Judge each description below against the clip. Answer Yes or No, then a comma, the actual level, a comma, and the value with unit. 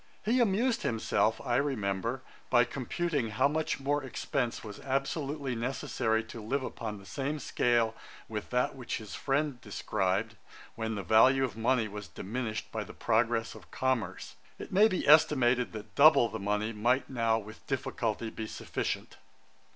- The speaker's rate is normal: Yes, average, 155 wpm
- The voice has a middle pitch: No, low, 120 Hz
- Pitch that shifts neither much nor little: Yes, average, 3.8 semitones